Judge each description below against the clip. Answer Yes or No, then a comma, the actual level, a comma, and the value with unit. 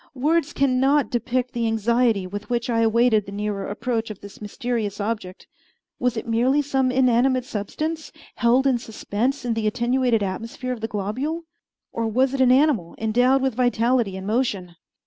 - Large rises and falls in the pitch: No, average, 3.2 semitones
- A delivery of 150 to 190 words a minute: Yes, average, 170 wpm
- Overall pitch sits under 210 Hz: No, high, 235 Hz